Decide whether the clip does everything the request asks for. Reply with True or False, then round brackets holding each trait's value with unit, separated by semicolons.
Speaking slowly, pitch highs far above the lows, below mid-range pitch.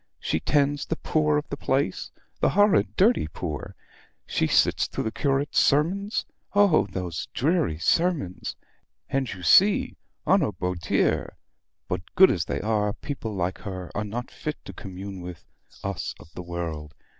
False (160 wpm; 9.0 semitones; 105 Hz)